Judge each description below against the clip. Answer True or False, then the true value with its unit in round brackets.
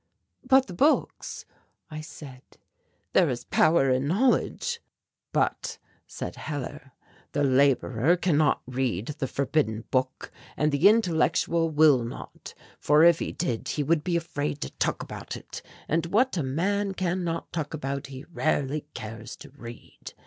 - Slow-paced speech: False (150 wpm)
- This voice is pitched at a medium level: True (150 Hz)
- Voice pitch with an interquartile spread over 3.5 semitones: True (4.3 semitones)